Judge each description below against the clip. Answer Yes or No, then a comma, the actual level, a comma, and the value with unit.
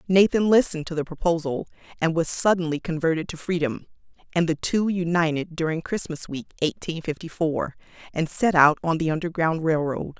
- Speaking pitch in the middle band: Yes, medium, 165 Hz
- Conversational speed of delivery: Yes, average, 170 wpm